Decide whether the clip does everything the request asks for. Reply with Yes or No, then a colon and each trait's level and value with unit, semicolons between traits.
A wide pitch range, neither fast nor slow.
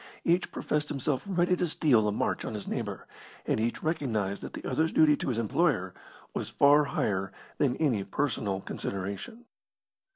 Yes: wide, 7.2 semitones; average, 165 wpm